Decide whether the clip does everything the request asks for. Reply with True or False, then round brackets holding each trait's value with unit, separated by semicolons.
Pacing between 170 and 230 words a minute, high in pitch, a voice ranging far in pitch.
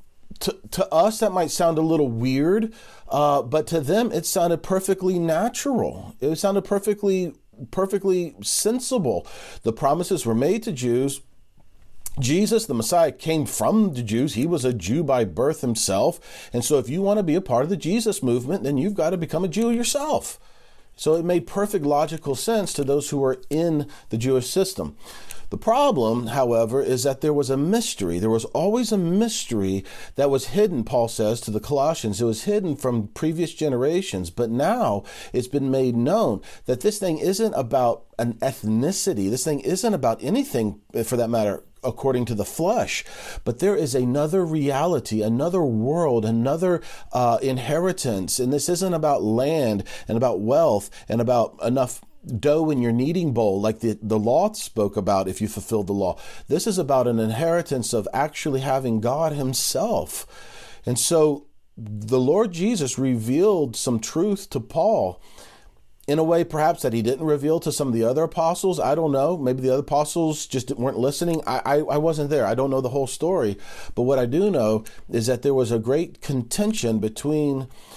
False (180 wpm; 145 Hz; 6.6 semitones)